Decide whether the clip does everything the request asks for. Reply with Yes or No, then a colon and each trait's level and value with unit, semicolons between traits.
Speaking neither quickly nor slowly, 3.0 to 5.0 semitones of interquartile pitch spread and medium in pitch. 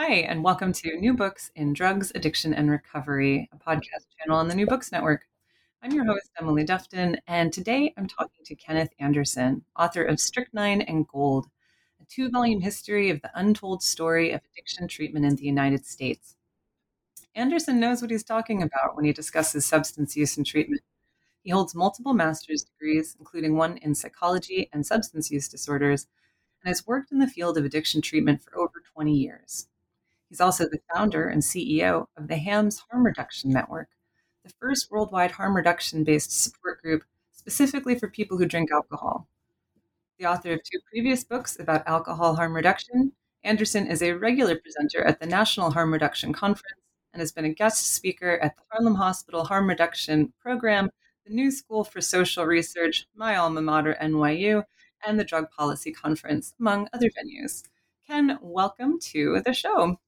No: average, 170 wpm; wide, 5.6 semitones; medium, 175 Hz